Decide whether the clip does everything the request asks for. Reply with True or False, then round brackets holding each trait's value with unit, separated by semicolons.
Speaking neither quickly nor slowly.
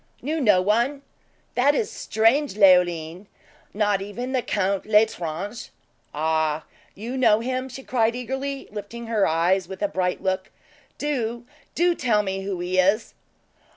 True (145 wpm)